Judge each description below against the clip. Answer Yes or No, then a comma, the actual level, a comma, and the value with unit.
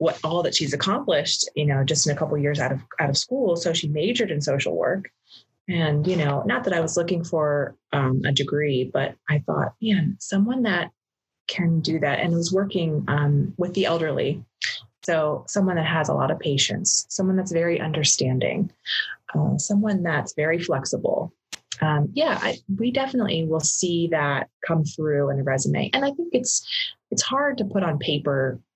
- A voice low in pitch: No, medium, 160 Hz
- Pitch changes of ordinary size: Yes, average, 4.3 semitones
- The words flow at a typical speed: Yes, average, 195 wpm